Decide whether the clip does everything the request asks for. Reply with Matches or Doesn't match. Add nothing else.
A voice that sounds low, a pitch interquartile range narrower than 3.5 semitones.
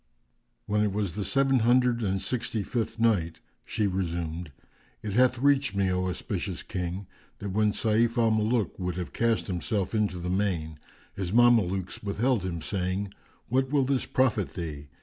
Doesn't match